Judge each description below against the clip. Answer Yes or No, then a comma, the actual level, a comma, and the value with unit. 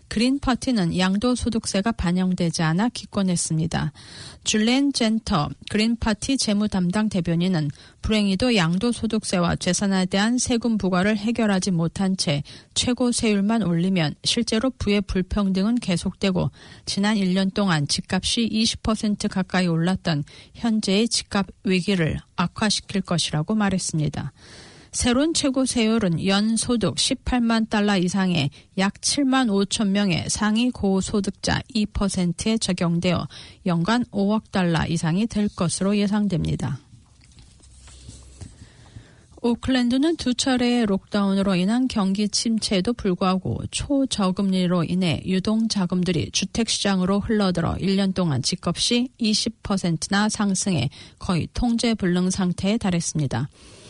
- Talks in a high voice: Yes, high, 195 Hz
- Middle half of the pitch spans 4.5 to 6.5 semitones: No, average, 3.9 semitones